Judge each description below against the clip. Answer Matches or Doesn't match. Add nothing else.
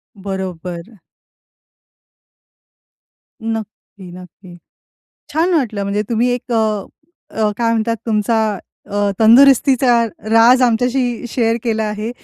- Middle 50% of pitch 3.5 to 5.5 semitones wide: Doesn't match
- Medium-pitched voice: Doesn't match